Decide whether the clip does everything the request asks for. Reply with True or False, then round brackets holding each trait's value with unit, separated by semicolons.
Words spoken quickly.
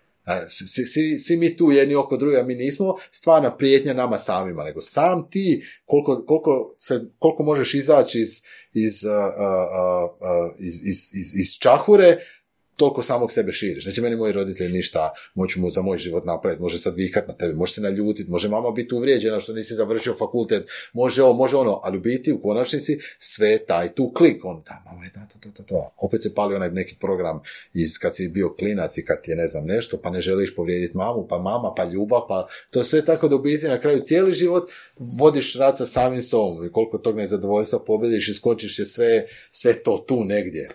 True (200 wpm)